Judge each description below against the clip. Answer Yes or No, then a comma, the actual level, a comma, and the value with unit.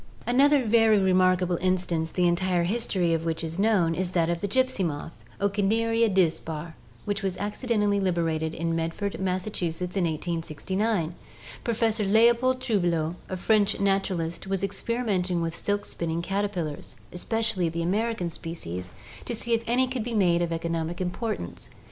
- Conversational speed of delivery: Yes, average, 150 wpm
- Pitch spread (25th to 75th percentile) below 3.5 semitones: No, average, 4.2 semitones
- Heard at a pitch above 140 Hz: Yes, medium, 185 Hz